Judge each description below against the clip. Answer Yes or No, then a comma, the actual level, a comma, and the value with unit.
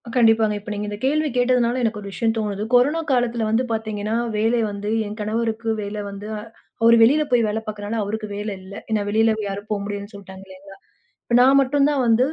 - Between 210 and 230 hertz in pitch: Yes, high, 220 Hz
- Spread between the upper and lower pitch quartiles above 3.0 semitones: No, narrow, 2.5 semitones